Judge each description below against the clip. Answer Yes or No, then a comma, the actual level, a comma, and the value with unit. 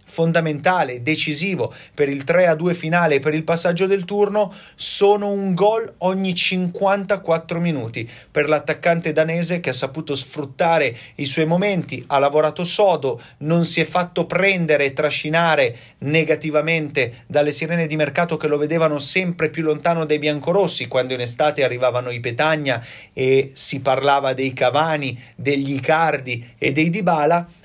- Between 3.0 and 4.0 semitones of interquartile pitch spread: Yes, average, 3.7 semitones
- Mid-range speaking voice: Yes, medium, 155 Hz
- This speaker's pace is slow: No, average, 145 wpm